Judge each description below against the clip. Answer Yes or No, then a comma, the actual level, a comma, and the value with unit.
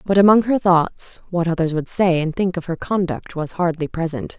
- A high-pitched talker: No, medium, 175 Hz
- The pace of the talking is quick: Yes, fast, 220 wpm